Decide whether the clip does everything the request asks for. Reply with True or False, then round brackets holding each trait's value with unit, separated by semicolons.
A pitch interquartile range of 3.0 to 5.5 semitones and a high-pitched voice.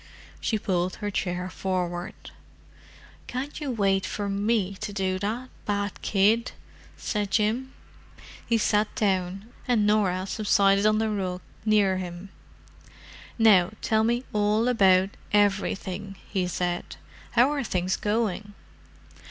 False (2.6 semitones; 205 Hz)